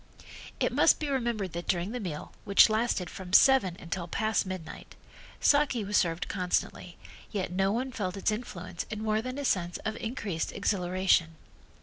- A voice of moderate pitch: No, high, 195 Hz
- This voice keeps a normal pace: Yes, average, 165 wpm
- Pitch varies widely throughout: No, average, 3.8 semitones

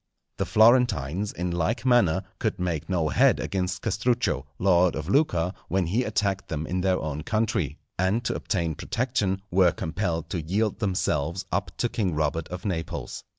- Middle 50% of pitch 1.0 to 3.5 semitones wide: No, average, 4.3 semitones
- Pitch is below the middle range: Yes, very low, 95 Hz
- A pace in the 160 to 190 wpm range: Yes, average, 165 wpm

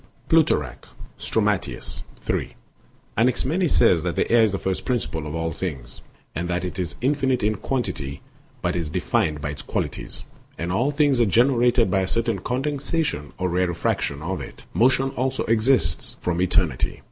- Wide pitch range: Yes, wide, 7.1 semitones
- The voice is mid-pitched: No, very low, 95 Hz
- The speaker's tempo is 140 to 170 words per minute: Yes, average, 165 wpm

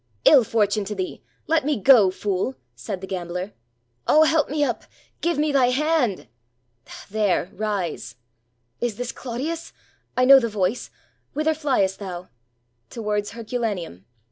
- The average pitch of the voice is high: Yes, high, 220 Hz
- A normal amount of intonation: No, wide, 6.3 semitones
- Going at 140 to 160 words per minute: Yes, average, 155 wpm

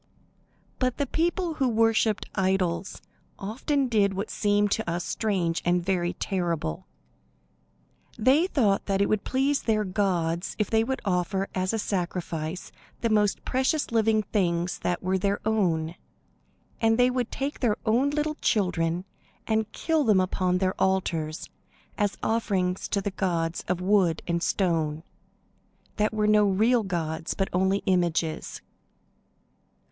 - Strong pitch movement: No, average, 3.9 semitones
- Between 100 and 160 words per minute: Yes, average, 140 wpm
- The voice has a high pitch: Yes, high, 195 Hz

